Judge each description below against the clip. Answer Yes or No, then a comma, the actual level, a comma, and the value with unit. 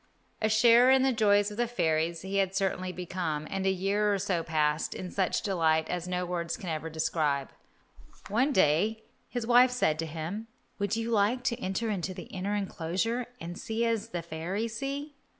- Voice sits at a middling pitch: No, high, 195 Hz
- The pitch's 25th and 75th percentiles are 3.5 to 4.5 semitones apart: No, average, 5.2 semitones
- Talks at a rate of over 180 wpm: Yes, average, 190 wpm